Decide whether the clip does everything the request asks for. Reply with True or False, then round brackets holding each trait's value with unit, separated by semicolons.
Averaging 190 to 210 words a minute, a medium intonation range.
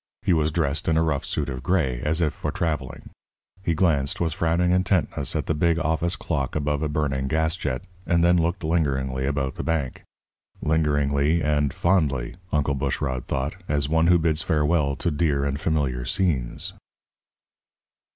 False (170 wpm; 3.0 semitones)